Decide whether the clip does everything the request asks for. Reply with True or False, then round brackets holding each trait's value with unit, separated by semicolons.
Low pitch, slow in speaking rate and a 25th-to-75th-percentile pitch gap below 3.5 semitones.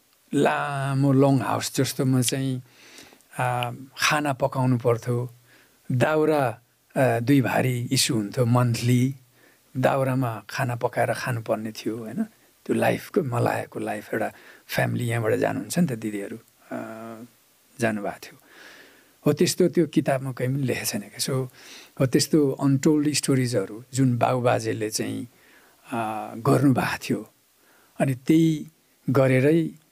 True (130 Hz; 110 wpm; 2.5 semitones)